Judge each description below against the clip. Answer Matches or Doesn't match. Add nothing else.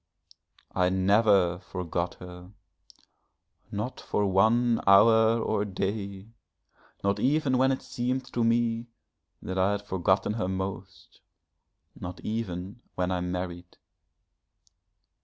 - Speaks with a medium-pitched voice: Doesn't match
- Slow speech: Matches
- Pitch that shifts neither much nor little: Matches